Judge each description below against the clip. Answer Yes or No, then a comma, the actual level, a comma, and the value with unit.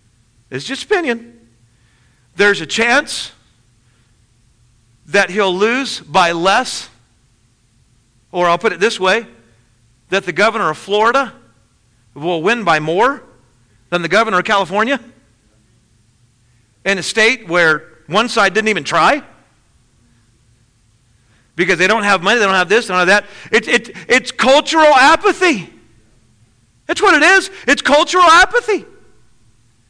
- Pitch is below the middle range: No, medium, 155 Hz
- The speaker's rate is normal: No, slow, 125 wpm